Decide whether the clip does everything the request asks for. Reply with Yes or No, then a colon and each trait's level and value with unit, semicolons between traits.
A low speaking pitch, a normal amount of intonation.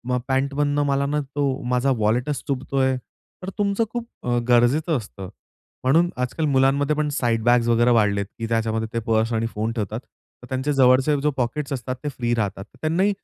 Yes: low, 130 Hz; average, 3.7 semitones